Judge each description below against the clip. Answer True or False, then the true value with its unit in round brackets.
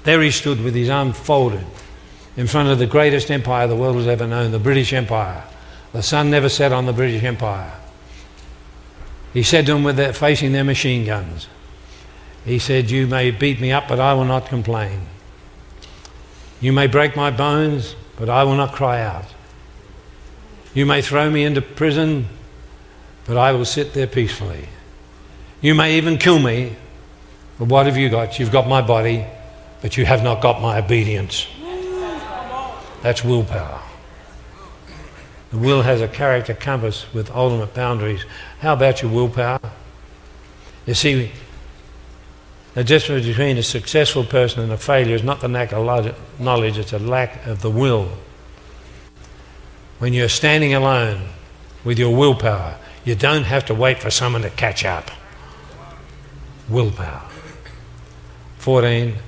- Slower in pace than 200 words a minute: True (155 wpm)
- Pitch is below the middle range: True (120 Hz)